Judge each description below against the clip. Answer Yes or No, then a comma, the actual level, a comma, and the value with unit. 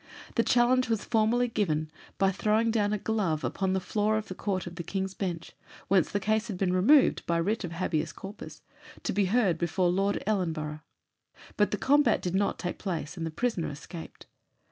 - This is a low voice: No, high, 195 Hz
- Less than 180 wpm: No, average, 190 wpm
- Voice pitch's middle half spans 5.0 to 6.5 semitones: No, average, 3.8 semitones